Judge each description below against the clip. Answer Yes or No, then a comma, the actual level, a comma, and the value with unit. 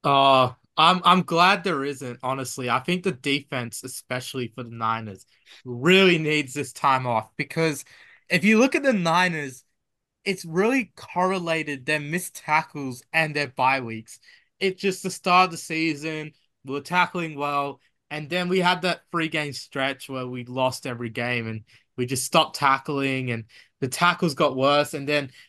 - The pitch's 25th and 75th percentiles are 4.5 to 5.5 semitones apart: Yes, average, 5.2 semitones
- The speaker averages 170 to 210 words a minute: Yes, average, 175 wpm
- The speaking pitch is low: No, medium, 145 Hz